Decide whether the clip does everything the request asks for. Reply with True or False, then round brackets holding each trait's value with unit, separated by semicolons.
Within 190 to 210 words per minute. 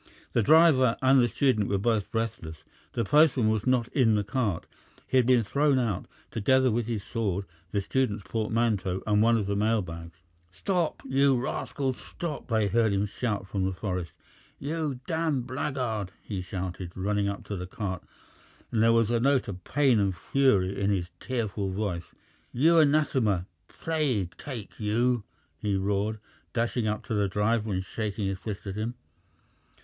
False (175 wpm)